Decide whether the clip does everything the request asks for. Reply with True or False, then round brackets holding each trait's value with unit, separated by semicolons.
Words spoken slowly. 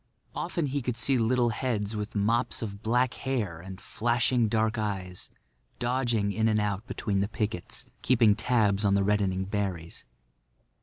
False (155 wpm)